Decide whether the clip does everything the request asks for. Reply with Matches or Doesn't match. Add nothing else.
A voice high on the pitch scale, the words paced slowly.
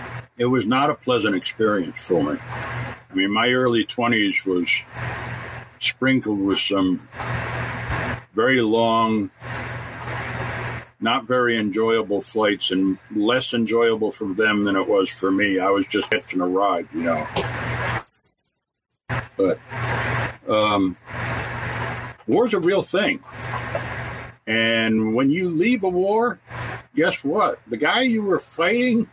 Doesn't match